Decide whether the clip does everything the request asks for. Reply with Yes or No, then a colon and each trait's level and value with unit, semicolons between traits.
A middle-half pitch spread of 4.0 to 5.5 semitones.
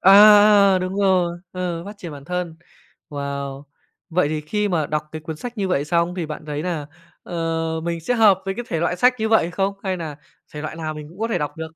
No: average, 3.3 semitones